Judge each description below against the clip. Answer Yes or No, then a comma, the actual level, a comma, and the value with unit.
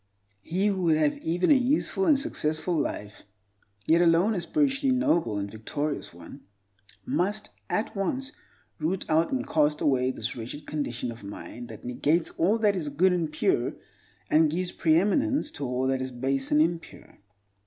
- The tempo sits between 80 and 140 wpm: No, average, 160 wpm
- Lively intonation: Yes, wide, 7.4 semitones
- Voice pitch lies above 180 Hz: No, medium, 155 Hz